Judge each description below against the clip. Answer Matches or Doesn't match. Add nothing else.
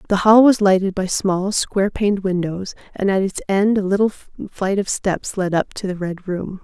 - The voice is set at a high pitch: Matches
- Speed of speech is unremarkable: Doesn't match